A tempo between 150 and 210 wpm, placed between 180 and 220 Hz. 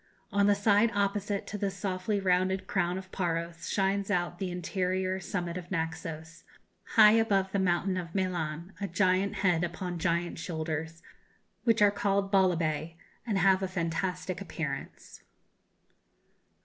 No: average, 140 wpm; medium, 185 Hz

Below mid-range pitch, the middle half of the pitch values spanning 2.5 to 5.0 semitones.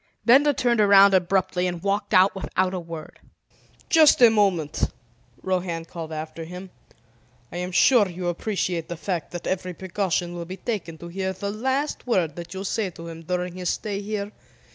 No: medium, 185 Hz; average, 2.8 semitones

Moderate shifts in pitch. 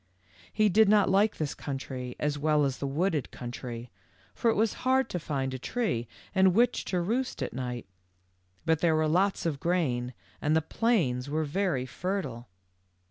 No: wide, 6.9 semitones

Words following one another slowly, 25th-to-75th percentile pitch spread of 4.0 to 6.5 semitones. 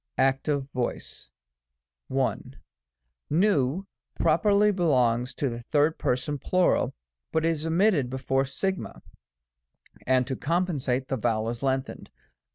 Yes: slow, 125 wpm; average, 4.4 semitones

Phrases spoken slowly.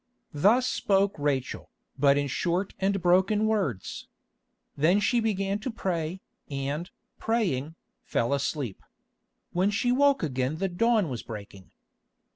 Yes: slow, 125 wpm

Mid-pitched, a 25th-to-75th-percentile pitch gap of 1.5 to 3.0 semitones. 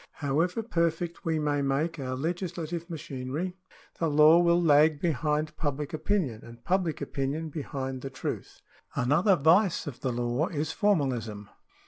No: medium, 155 Hz; average, 3.9 semitones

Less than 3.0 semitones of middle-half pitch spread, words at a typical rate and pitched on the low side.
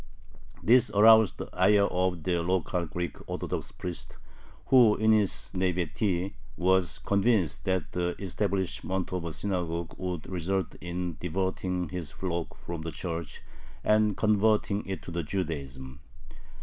No: narrow, 2.6 semitones; slow, 130 wpm; very low, 90 Hz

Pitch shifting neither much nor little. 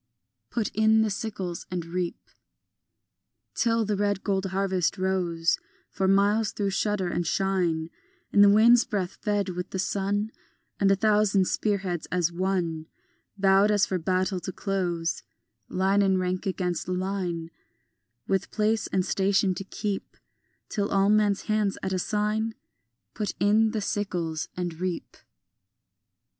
No: narrow, 2.2 semitones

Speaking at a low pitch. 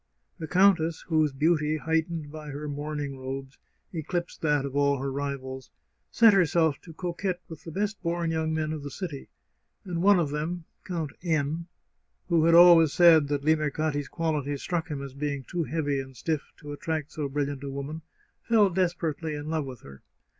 No: medium, 155 Hz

